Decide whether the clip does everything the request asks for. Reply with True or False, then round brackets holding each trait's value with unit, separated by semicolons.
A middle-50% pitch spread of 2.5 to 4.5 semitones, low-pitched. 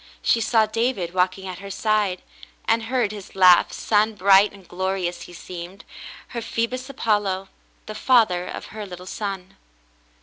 False (3.3 semitones; 200 Hz)